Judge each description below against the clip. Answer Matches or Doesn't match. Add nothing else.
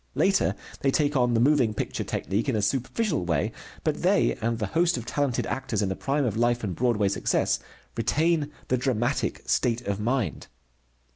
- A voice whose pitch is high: Doesn't match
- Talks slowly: Doesn't match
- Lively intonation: Doesn't match